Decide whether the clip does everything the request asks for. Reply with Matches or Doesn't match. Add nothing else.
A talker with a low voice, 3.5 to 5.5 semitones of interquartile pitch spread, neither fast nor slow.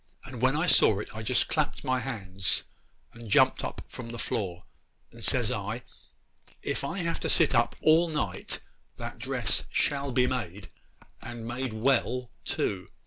Matches